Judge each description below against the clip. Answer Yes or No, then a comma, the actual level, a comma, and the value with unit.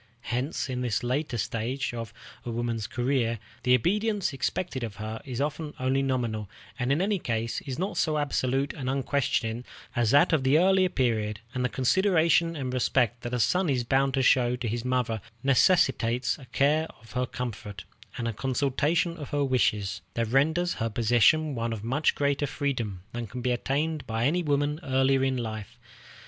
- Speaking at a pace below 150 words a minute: No, average, 185 wpm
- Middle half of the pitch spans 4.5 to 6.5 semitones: No, average, 3.7 semitones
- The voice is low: Yes, low, 130 Hz